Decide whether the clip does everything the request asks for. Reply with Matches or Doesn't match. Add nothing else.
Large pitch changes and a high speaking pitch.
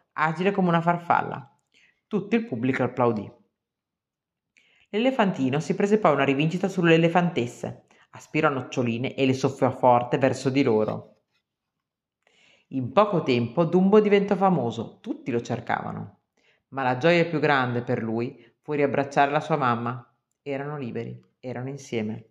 Doesn't match